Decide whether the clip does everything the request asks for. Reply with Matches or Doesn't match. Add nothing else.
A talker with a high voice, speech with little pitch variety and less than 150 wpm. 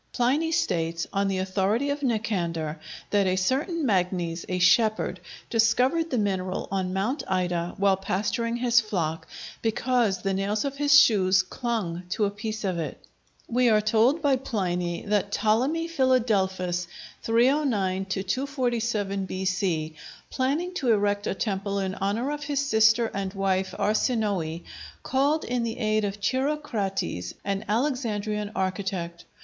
Doesn't match